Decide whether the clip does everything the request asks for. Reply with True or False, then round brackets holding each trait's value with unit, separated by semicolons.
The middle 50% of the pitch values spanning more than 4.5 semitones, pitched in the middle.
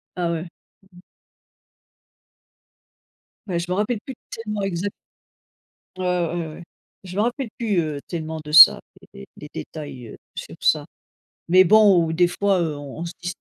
False (3.9 semitones; 175 Hz)